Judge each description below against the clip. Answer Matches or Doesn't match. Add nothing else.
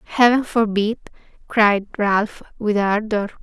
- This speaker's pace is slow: Matches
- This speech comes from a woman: Matches